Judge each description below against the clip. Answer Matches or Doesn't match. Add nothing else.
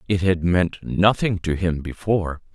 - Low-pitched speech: Matches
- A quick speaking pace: Doesn't match